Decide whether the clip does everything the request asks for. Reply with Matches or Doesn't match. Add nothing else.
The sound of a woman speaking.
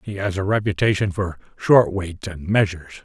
Doesn't match